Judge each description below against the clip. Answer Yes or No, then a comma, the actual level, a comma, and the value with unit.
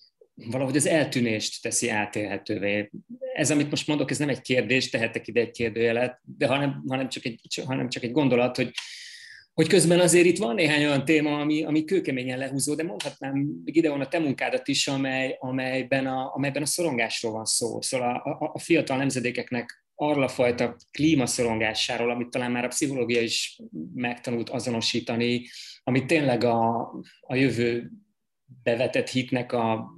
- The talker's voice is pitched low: Yes, low, 130 Hz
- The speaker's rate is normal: No, fast, 165 wpm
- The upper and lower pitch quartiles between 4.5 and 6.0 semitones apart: No, average, 3.8 semitones